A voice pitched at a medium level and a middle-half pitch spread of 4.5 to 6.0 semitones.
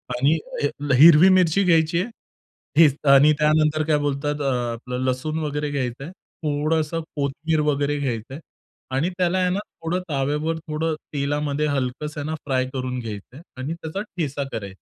No: medium, 150 Hz; average, 2.7 semitones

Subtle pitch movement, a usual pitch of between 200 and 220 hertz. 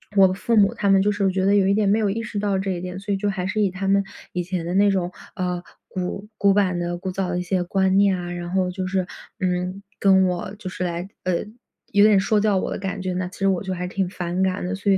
No: narrow, 1.6 semitones; high, 190 Hz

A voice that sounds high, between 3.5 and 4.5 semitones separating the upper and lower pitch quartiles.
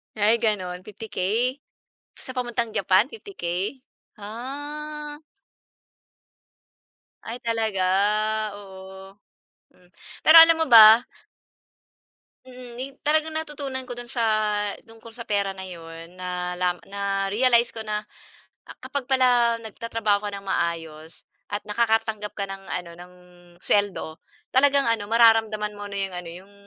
Yes: high, 220 Hz; average, 4.2 semitones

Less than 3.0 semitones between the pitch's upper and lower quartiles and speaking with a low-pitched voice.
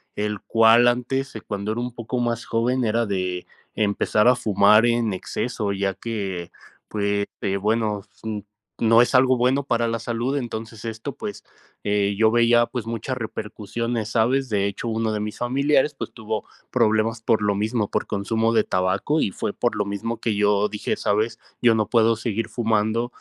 Yes: narrow, 2.4 semitones; low, 115 Hz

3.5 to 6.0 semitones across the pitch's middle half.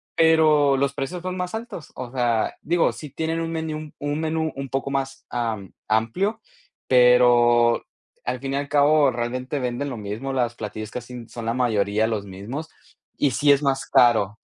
Yes: average, 4.1 semitones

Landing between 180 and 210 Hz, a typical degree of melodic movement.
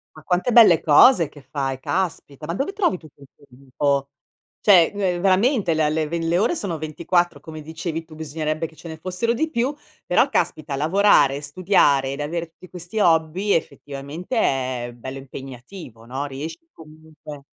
No: medium, 160 Hz; average, 4.4 semitones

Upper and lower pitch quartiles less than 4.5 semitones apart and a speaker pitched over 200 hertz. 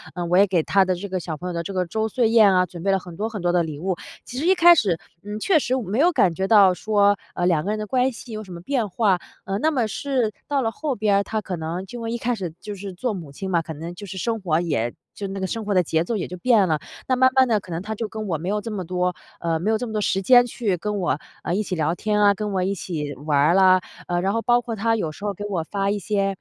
No: average, 3.8 semitones; high, 195 Hz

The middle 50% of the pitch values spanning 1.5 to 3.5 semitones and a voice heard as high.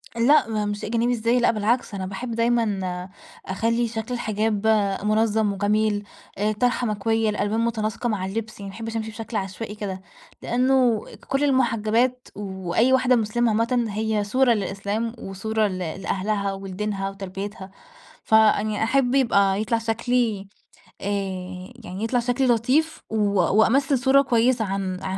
Yes: average, 3.0 semitones; high, 220 Hz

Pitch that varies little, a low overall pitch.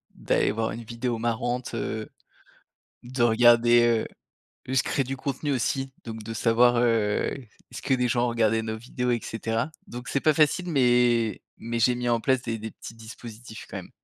Yes: narrow, 1.6 semitones; low, 120 Hz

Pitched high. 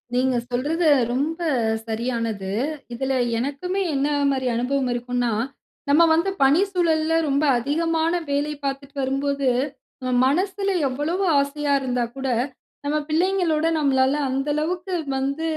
Yes: very high, 280 Hz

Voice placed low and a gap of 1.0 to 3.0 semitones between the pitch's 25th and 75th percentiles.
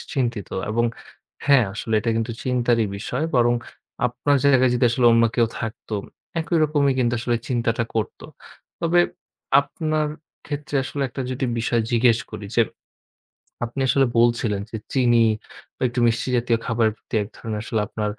Yes: low, 120 Hz; narrow, 2.5 semitones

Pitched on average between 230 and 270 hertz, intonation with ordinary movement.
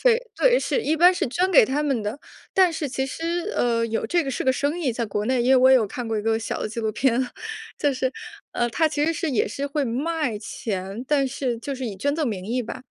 Yes: very high, 260 Hz; average, 5.0 semitones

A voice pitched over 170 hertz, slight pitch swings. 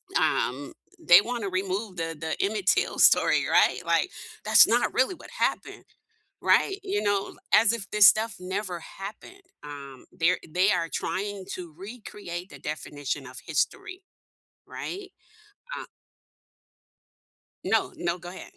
No: high, 190 Hz; average, 4.2 semitones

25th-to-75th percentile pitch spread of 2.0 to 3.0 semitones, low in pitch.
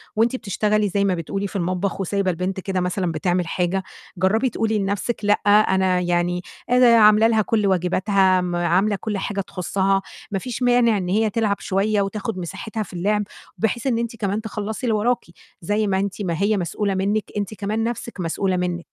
No: narrow, 2.6 semitones; high, 200 Hz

